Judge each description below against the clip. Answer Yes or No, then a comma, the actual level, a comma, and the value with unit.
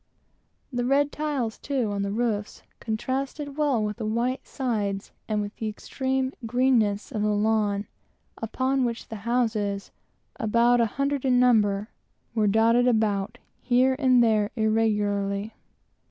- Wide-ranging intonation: No, average, 3.4 semitones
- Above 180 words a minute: No, average, 140 wpm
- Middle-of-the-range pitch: No, high, 225 Hz